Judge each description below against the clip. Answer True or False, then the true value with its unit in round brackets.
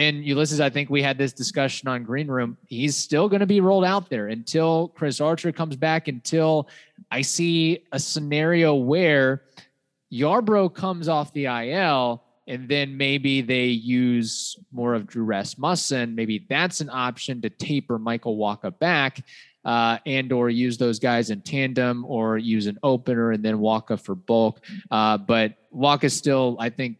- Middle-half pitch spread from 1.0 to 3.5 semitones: False (4.3 semitones)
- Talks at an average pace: True (170 wpm)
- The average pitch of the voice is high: False (135 Hz)